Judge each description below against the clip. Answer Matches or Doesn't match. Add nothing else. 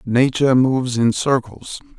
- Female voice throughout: Doesn't match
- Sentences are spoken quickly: Doesn't match